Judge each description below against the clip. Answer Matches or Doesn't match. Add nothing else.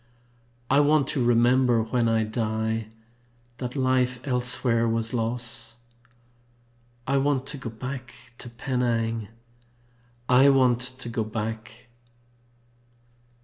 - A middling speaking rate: Doesn't match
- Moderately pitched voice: Doesn't match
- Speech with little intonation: Matches